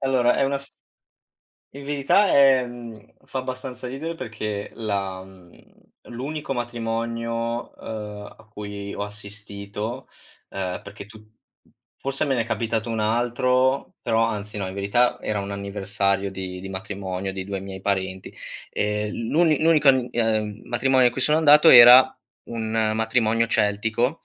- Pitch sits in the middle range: No, low, 110 Hz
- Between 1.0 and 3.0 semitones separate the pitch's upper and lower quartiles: No, average, 3.9 semitones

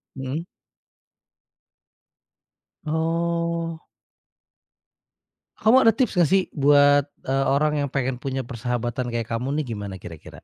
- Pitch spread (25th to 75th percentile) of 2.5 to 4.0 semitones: No, average, 4.9 semitones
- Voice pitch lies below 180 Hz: Yes, medium, 140 Hz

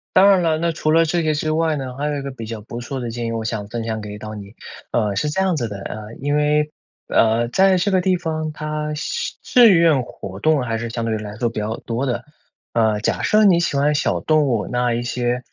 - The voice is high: No, low, 135 Hz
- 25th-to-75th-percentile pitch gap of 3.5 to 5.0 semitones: No, wide, 5.5 semitones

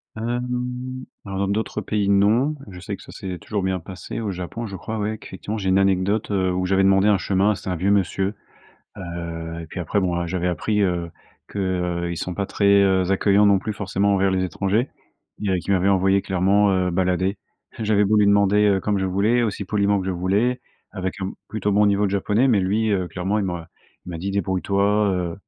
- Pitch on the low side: Yes, low, 100 Hz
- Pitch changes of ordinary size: No, narrow, 1.9 semitones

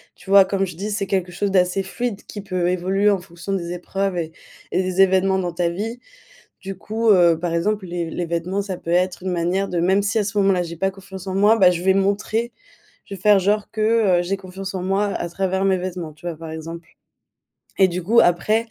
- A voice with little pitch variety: Yes, narrow, 2.1 semitones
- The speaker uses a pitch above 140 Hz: Yes, high, 190 Hz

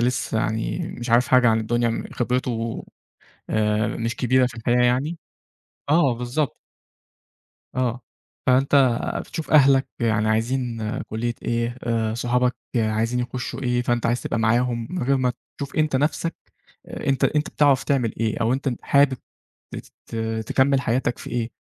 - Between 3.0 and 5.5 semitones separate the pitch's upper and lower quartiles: No, narrow, 2.4 semitones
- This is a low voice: Yes, low, 125 Hz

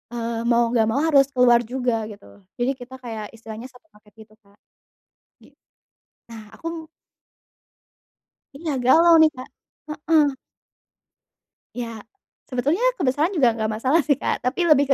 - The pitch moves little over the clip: No, average, 4.6 semitones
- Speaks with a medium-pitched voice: No, very high, 250 Hz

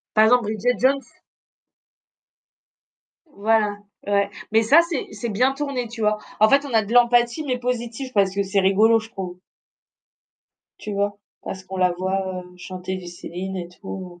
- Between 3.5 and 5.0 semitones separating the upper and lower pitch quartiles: Yes, average, 4.2 semitones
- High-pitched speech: Yes, high, 210 Hz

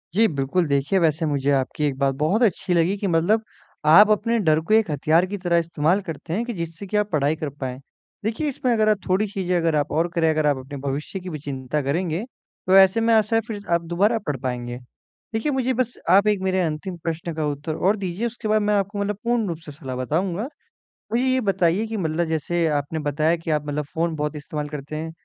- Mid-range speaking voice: Yes, medium, 170 Hz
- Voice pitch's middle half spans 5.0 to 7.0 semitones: Yes, wide, 5.4 semitones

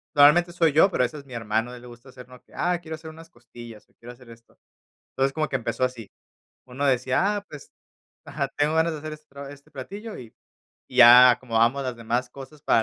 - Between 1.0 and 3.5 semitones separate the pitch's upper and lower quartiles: No, average, 4.1 semitones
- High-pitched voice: No, low, 135 Hz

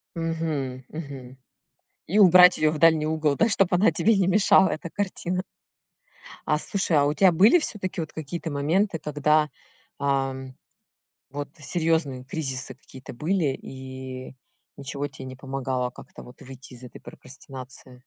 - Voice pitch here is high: No, medium, 150 Hz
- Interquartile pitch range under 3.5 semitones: No, average, 4.4 semitones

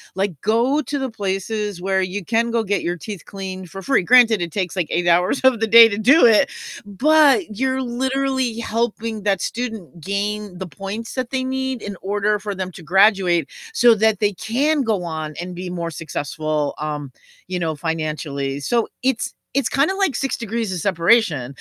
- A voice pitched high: Yes, high, 205 Hz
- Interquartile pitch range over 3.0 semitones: Yes, average, 5.0 semitones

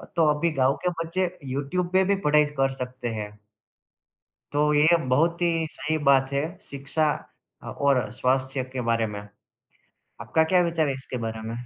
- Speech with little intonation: No, average, 3.8 semitones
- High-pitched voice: No, medium, 140 Hz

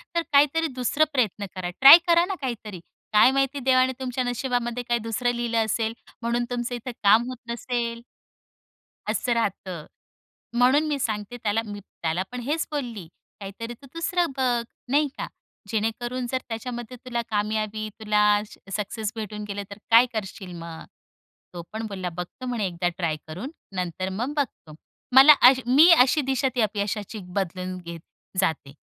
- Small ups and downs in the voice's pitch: No, average, 3.8 semitones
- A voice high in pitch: Yes, high, 230 Hz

